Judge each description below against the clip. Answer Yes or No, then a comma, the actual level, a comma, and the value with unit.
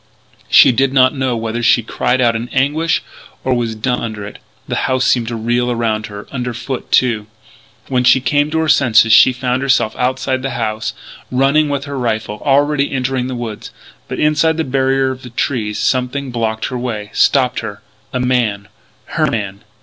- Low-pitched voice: Yes, low, 125 Hz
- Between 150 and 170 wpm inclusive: No, average, 185 wpm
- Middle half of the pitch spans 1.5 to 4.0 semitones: Yes, average, 2.9 semitones